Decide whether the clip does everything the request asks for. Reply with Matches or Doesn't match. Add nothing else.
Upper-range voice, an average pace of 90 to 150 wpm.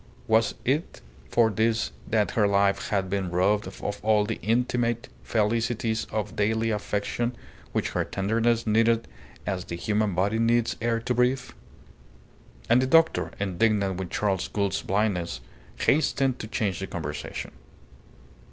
Doesn't match